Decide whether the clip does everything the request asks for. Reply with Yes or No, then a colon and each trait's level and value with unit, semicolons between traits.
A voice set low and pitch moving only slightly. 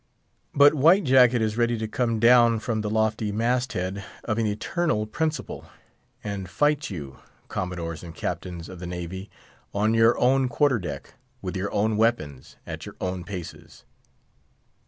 No: low, 110 Hz; average, 4.8 semitones